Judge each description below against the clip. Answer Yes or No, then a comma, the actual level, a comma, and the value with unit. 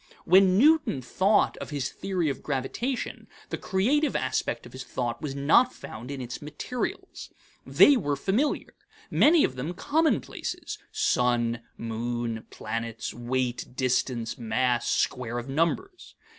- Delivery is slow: Yes, slow, 130 wpm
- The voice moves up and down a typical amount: No, wide, 8.4 semitones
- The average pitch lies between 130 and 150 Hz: Yes, low, 135 Hz